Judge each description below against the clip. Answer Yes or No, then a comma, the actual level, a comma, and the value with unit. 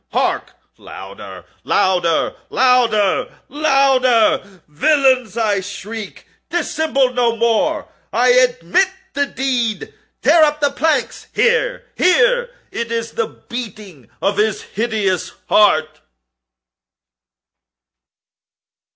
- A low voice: No, high, 245 Hz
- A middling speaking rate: No, slow, 80 wpm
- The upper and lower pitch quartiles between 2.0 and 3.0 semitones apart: No, average, 5.3 semitones